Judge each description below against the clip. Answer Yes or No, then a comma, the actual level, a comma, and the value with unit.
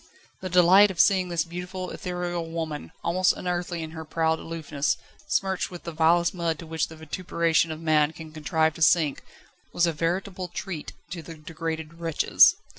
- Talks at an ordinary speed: Yes, average, 175 wpm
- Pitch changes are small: Yes, narrow, 1.9 semitones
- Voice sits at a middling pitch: Yes, medium, 165 Hz